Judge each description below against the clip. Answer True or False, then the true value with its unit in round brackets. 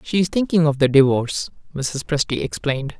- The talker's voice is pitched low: False (150 Hz)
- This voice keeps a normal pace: True (180 wpm)